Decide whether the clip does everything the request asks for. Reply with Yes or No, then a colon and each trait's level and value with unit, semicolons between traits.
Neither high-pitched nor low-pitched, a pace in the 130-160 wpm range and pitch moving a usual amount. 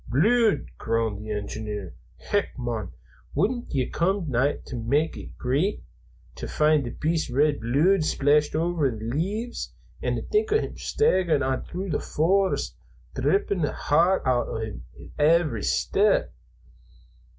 No: medium, 150 Hz; average, 145 wpm; wide, 7.3 semitones